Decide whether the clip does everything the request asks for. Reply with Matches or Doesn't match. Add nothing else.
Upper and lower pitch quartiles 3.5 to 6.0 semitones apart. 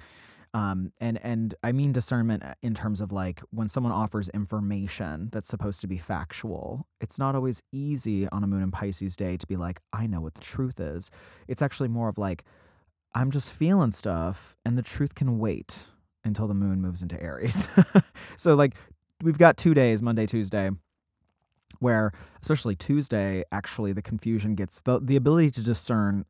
Matches